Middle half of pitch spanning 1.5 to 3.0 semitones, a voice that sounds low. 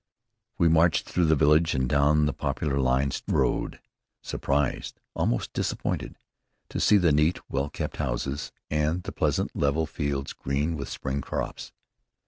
Yes: narrow, 2.5 semitones; very low, 75 Hz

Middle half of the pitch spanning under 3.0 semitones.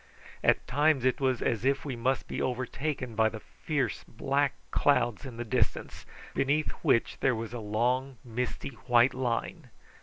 Yes: narrow, 2.6 semitones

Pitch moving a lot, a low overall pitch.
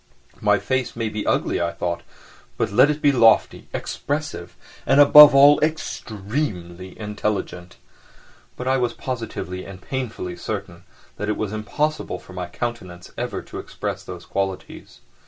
Yes: wide, 6.6 semitones; low, 110 Hz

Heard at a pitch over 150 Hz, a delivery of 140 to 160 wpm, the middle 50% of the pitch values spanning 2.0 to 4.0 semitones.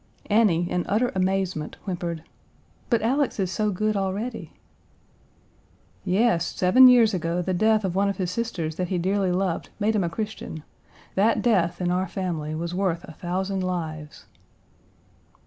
Yes: medium, 185 Hz; average, 155 wpm; average, 3.4 semitones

